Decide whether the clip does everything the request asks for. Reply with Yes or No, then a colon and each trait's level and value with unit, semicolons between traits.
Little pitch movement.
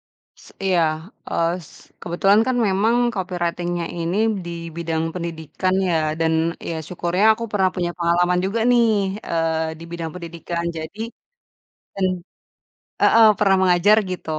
Yes: narrow, 2.3 semitones